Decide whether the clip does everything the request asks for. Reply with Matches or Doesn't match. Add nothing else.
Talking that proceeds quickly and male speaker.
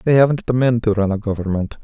Matches